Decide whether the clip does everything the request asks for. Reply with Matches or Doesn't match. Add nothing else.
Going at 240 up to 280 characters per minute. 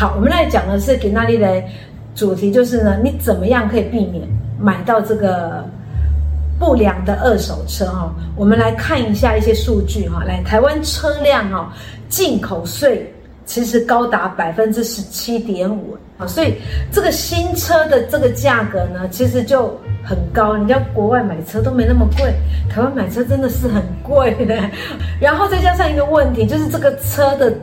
Matches